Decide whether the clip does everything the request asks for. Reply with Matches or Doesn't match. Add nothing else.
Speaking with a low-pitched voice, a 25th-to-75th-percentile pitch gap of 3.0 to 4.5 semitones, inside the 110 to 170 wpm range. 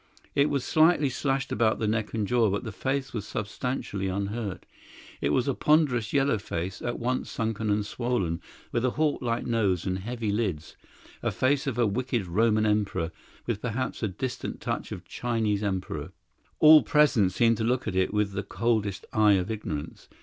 Doesn't match